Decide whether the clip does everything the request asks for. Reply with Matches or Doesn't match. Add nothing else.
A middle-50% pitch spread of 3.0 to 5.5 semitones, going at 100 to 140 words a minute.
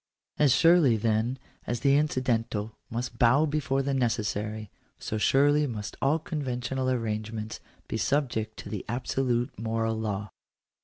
Matches